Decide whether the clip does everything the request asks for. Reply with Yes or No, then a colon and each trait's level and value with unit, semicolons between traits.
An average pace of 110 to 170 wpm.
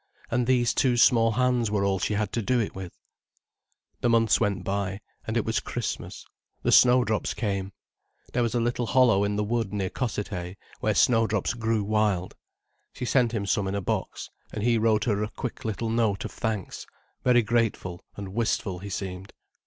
No: average, 180 wpm